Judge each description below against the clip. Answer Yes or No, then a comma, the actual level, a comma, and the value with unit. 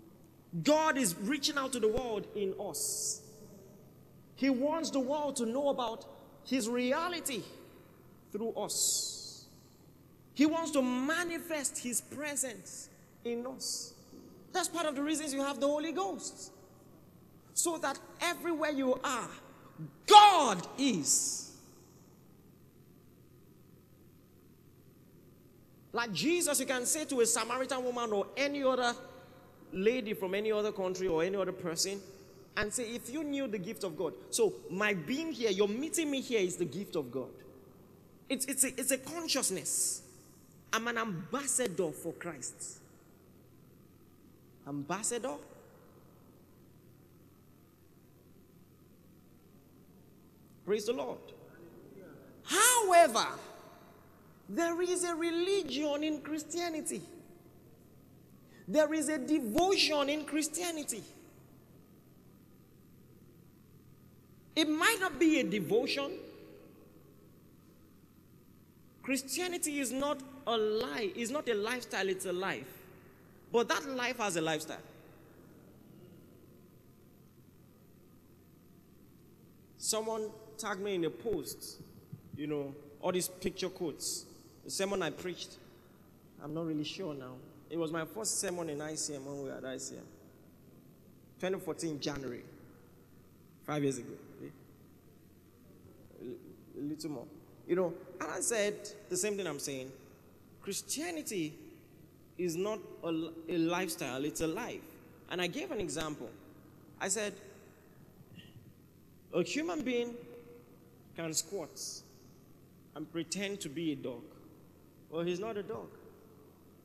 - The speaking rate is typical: No, slow, 115 wpm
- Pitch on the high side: Yes, high, 225 Hz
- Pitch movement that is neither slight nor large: No, wide, 8.3 semitones